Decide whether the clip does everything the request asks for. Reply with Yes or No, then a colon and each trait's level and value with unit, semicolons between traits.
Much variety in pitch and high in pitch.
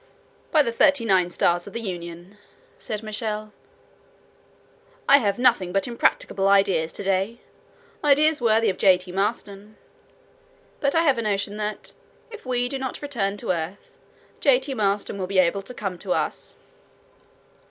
No: average, 4.1 semitones; high, 210 Hz